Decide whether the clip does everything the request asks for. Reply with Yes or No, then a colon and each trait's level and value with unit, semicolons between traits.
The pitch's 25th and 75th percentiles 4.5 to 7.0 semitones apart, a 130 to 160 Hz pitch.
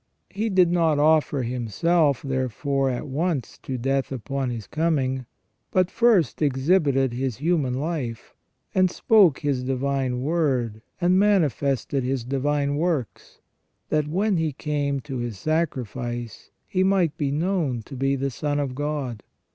No: average, 4.0 semitones; medium, 140 Hz